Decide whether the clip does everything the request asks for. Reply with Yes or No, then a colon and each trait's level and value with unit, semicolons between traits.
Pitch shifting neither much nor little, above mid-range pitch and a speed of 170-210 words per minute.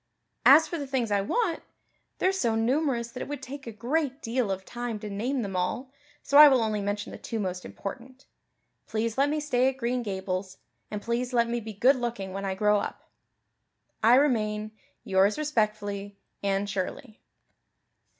Yes: average, 4.5 semitones; high, 230 Hz; average, 180 wpm